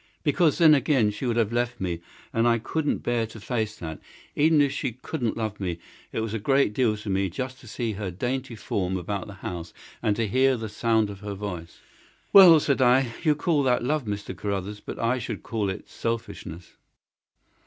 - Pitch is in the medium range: No, low, 115 Hz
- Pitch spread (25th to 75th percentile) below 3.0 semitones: No, average, 4.2 semitones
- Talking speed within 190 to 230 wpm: Yes, fast, 205 wpm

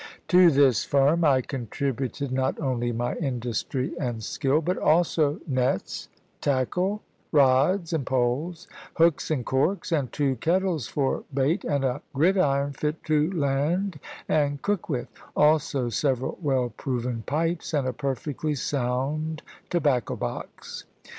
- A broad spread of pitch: No, average, 3.6 semitones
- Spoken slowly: Yes, slow, 130 wpm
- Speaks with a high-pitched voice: No, medium, 140 Hz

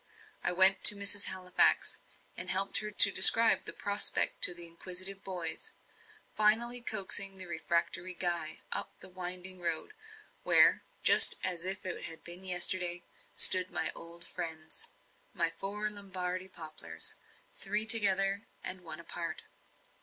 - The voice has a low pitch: No, medium, 185 Hz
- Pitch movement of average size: No, narrow, 2.3 semitones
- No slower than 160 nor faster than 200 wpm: No, average, 140 wpm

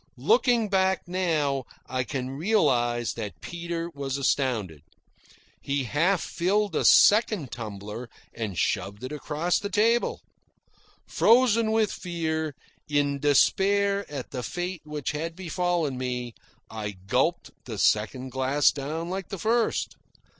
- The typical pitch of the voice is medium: Yes, medium, 150 Hz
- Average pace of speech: No, slow, 125 wpm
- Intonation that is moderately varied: No, wide, 6.7 semitones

